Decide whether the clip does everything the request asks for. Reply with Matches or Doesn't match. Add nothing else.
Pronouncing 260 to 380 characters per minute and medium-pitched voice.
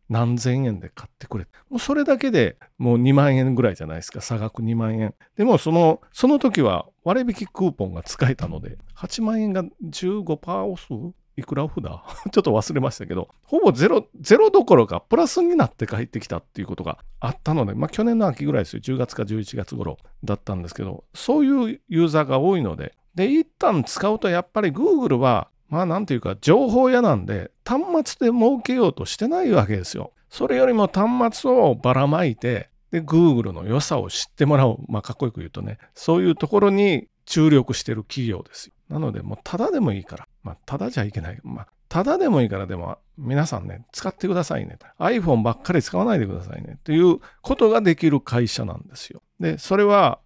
Doesn't match